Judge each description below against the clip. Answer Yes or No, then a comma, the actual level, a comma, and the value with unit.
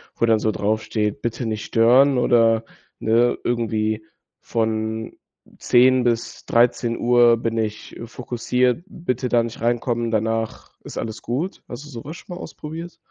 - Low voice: Yes, low, 115 Hz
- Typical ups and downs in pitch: No, narrow, 1.8 semitones